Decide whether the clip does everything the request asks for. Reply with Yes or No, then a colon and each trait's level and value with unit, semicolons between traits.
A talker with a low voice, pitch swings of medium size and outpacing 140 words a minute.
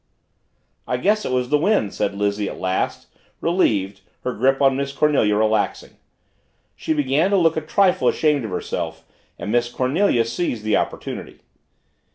No: low, 130 Hz; wide, 6.7 semitones; average, 160 wpm